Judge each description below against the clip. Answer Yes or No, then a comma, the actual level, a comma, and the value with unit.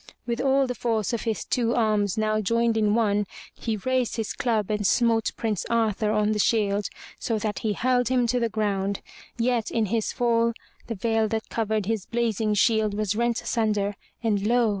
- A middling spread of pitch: No, narrow, 1.8 semitones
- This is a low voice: No, high, 220 Hz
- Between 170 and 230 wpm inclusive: Yes, average, 190 wpm